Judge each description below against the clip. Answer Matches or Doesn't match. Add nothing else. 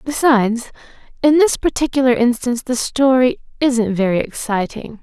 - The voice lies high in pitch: Matches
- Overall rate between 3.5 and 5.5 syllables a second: Matches